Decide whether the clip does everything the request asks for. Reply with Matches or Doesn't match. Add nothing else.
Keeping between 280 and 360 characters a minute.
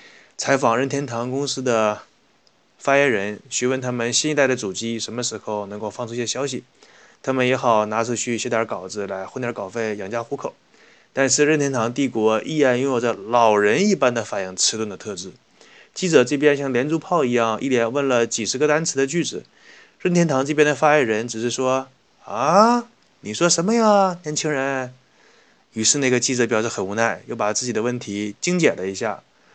Matches